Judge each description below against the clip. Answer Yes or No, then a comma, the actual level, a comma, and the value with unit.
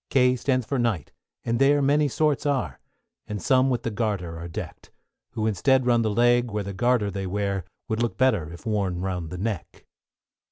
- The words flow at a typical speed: Yes, average, 195 wpm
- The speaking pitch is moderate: No, low, 110 Hz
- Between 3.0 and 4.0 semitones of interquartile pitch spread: No, average, 4.6 semitones